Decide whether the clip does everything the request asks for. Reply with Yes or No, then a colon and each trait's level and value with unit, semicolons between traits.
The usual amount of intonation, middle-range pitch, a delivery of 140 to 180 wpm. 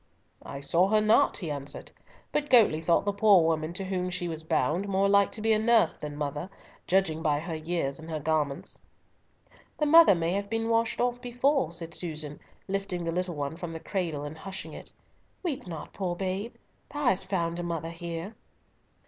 No: average, 4.0 semitones; medium, 175 Hz; average, 190 wpm